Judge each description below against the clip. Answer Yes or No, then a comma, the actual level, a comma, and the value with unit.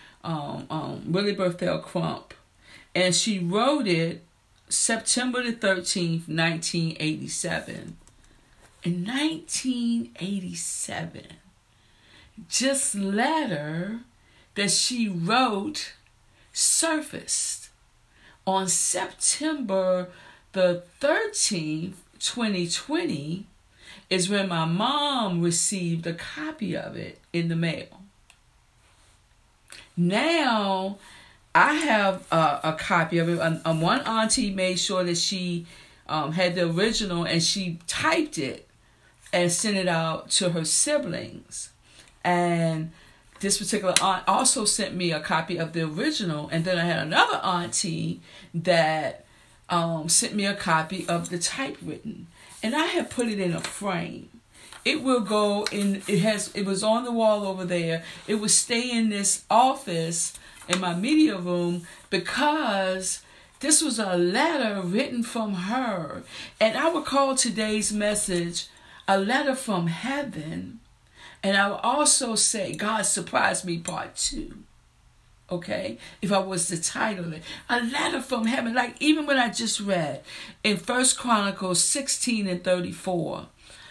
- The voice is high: Yes, high, 195 Hz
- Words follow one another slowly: Yes, slow, 130 wpm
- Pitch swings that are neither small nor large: Yes, average, 4.9 semitones